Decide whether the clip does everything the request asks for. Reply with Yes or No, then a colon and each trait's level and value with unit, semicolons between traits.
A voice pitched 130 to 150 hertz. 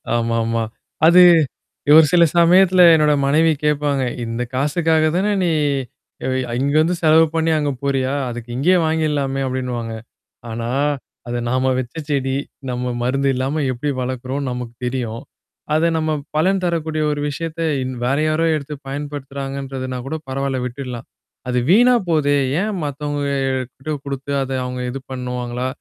Yes: medium, 140 Hz